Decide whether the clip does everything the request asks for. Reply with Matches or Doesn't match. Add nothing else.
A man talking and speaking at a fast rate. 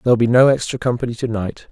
Matches